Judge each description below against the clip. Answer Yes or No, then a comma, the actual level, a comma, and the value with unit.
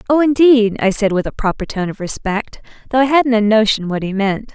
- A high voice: Yes, high, 225 Hz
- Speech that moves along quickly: Yes, fast, 240 wpm